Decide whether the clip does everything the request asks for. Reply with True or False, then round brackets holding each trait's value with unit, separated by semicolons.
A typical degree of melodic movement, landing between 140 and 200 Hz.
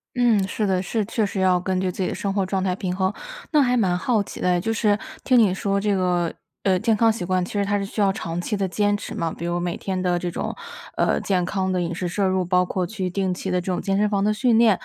False (2.3 semitones; 190 Hz)